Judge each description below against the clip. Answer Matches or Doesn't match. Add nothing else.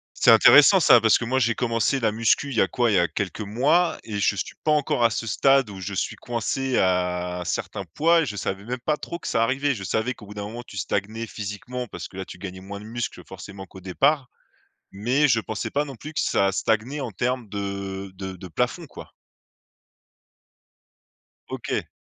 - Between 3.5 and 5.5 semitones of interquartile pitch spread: Matches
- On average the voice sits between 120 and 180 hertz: Doesn't match